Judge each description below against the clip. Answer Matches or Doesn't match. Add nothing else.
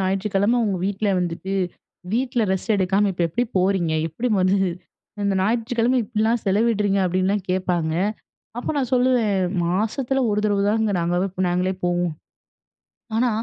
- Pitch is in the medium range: Doesn't match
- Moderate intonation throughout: Matches